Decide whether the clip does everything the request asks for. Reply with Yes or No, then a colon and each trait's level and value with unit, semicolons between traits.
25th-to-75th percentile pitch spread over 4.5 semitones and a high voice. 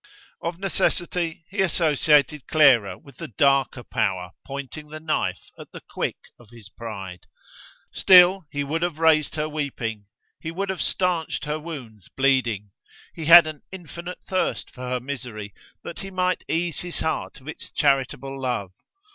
No: average, 5.1 semitones; medium, 150 Hz